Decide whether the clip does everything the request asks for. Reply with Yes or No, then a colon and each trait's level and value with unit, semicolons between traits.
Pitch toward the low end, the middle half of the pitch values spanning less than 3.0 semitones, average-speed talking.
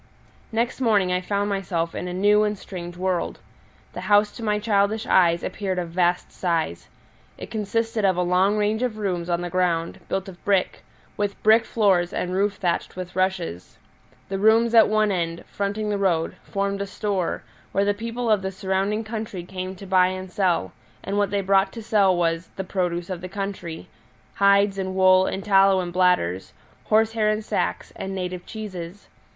No: high, 195 Hz; narrow, 2.4 semitones; average, 185 wpm